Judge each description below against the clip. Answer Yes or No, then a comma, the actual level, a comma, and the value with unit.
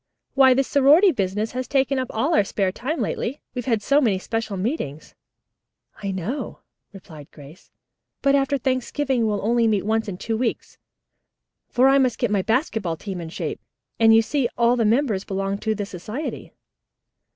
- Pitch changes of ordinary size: Yes, average, 5.0 semitones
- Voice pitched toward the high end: Yes, high, 225 Hz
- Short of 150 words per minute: No, average, 180 wpm